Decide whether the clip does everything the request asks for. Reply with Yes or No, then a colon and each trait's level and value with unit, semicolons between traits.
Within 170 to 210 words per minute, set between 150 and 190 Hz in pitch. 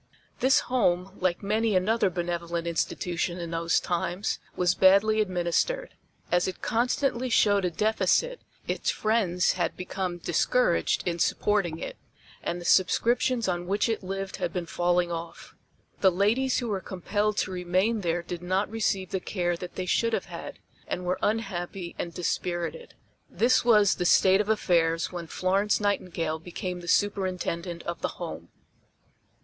No: average, 155 wpm; medium, 185 Hz